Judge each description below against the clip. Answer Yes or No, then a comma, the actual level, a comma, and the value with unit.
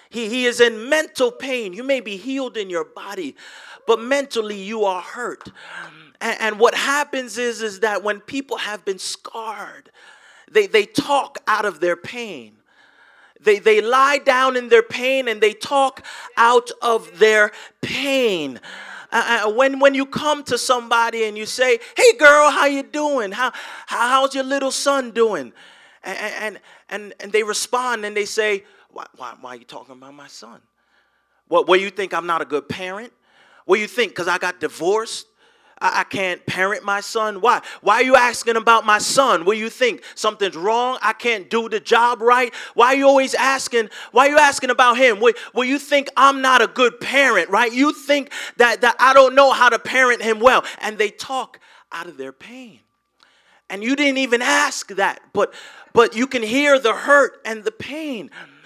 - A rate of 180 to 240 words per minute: Yes, average, 195 wpm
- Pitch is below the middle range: No, high, 240 Hz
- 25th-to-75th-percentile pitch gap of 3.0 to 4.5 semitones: Yes, average, 4.1 semitones